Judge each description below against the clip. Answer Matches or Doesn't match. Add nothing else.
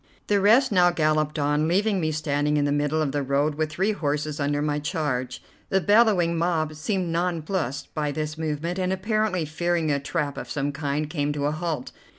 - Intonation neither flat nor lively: Matches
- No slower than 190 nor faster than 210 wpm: Matches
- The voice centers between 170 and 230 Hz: Doesn't match